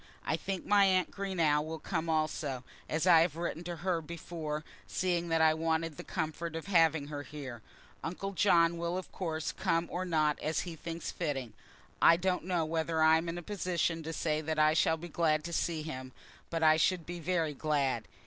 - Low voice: No, medium, 165 Hz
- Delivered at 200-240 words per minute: Yes, fast, 205 wpm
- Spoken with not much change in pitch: Yes, narrow, 1.9 semitones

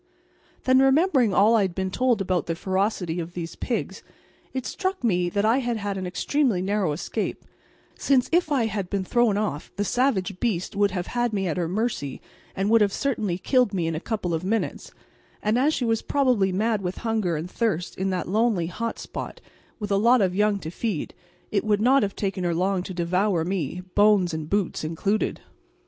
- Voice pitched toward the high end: Yes, high, 200 Hz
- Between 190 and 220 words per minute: Yes, fast, 205 wpm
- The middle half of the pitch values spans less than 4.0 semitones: No, average, 4.3 semitones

